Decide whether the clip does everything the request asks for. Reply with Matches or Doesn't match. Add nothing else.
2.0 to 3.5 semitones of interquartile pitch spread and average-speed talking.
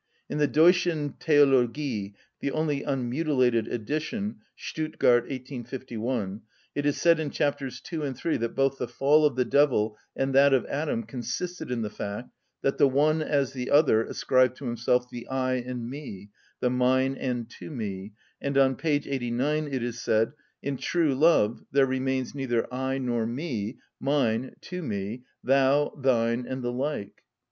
Matches